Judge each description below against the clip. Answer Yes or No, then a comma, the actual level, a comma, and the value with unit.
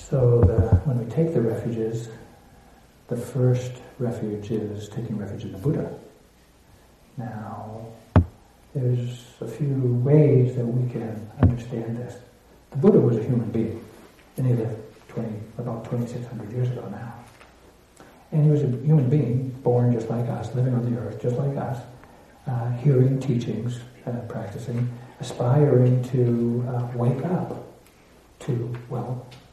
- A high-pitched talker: No, low, 120 Hz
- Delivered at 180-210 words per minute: No, average, 140 wpm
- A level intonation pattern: Yes, narrow, 1.8 semitones